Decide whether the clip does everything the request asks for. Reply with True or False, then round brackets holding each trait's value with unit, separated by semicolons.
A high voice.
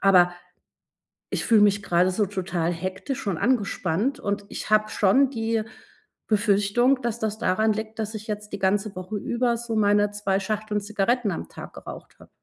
True (210 Hz)